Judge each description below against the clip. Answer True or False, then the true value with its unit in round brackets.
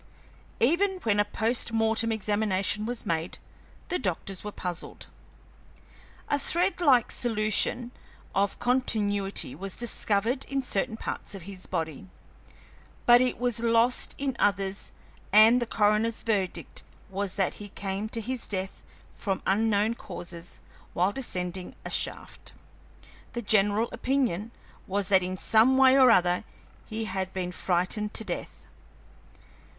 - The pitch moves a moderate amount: True (3.7 semitones)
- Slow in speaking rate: True (130 wpm)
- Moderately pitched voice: False (210 Hz)